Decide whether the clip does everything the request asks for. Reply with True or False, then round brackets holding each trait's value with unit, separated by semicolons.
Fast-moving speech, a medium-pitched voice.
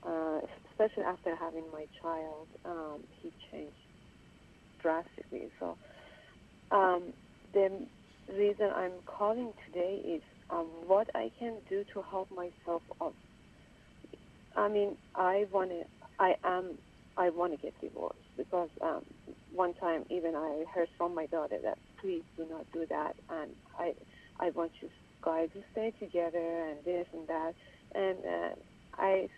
False (145 wpm; 175 Hz)